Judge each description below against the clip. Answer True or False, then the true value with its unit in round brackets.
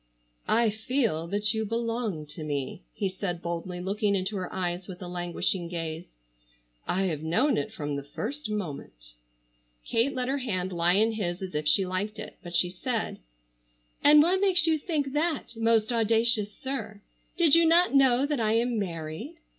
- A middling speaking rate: True (180 wpm)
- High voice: True (210 Hz)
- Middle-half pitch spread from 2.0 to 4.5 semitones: False (5.6 semitones)